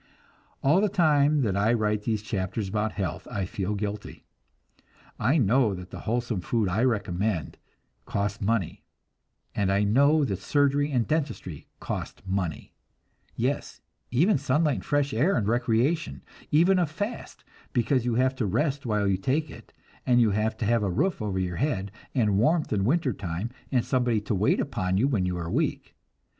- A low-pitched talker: Yes, low, 115 Hz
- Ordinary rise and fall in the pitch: No, wide, 5.7 semitones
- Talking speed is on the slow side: No, average, 175 wpm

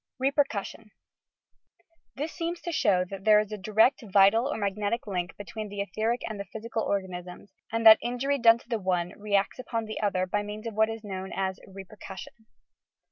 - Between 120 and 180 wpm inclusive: No, average, 195 wpm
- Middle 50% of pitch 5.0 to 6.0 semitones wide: No, average, 2.8 semitones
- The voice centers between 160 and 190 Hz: No, high, 215 Hz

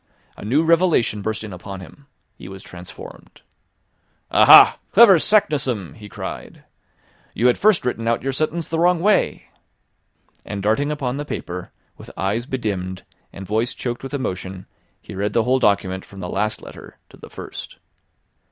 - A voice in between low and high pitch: No, low, 115 Hz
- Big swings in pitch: Yes, wide, 6.9 semitones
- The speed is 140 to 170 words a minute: Yes, average, 160 wpm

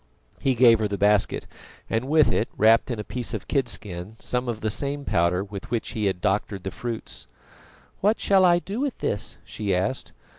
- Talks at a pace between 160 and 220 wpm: Yes, average, 195 wpm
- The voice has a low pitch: Yes, low, 110 Hz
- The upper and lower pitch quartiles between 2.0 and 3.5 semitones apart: No, average, 4.8 semitones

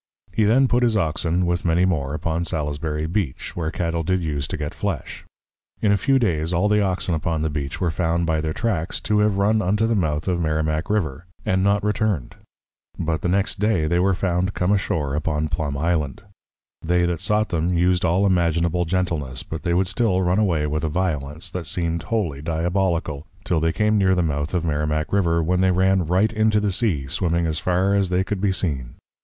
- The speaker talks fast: Yes, fast, 210 wpm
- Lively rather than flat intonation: No, average, 3.6 semitones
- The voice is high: No, very low, 85 Hz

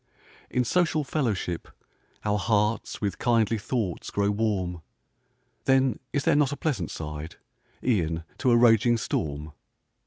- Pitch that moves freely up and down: Yes, wide, 5.9 semitones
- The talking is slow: Yes, slow, 130 wpm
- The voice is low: Yes, low, 110 Hz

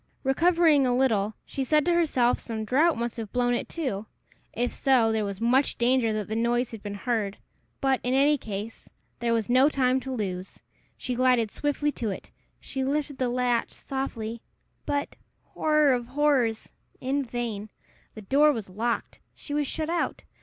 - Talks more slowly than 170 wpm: No, average, 175 wpm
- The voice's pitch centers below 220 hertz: No, very high, 250 Hz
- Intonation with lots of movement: No, average, 3.7 semitones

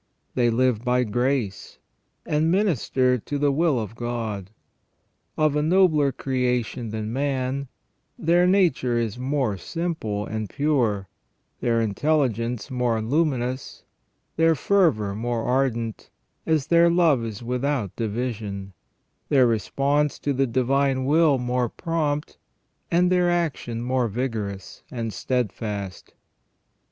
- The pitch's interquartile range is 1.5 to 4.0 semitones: No, average, 4.4 semitones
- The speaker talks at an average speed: No, slow, 120 wpm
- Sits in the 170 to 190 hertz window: No, low, 125 Hz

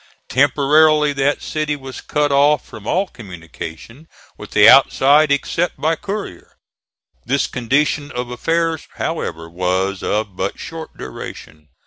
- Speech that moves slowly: Yes, slow, 125 wpm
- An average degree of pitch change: No, wide, 7.5 semitones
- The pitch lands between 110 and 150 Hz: Yes, medium, 140 Hz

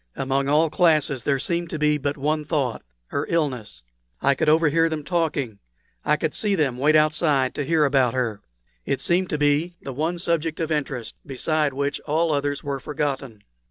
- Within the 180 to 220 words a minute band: Yes, average, 185 wpm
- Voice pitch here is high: No, medium, 150 Hz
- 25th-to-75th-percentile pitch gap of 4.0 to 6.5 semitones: No, average, 2.7 semitones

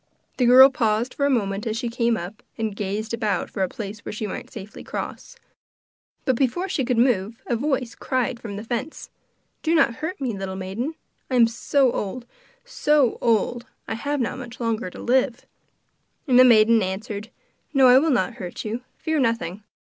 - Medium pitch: No, high, 235 Hz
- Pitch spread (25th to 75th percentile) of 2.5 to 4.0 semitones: Yes, average, 3.4 semitones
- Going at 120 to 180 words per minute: No, average, 190 wpm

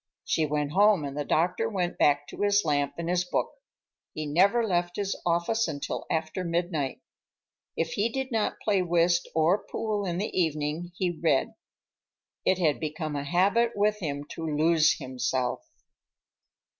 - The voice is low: No, medium, 170 Hz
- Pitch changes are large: No, average, 4.5 semitones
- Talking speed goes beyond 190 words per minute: No, average, 160 wpm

